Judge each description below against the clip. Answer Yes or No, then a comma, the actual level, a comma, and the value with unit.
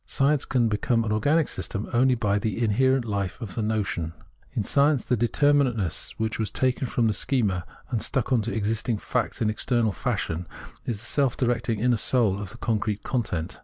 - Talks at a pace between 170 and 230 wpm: Yes, average, 195 wpm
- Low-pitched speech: Yes, low, 115 Hz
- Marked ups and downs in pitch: No, average, 3.3 semitones